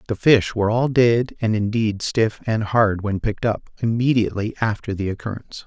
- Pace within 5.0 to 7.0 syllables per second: Yes, 5.5 syllables/s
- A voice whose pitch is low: Yes, low, 110 Hz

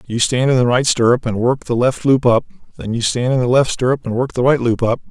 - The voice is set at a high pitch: No, low, 125 Hz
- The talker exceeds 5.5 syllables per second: Yes, 5.9 syllables/s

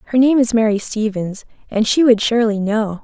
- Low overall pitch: No, high, 225 Hz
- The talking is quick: No, average, 195 wpm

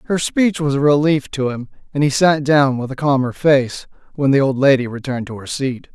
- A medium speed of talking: No, fast, 230 wpm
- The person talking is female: No, male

